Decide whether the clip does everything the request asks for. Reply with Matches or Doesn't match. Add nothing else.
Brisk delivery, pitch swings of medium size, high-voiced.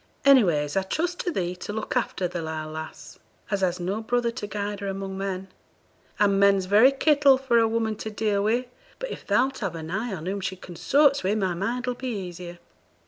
Matches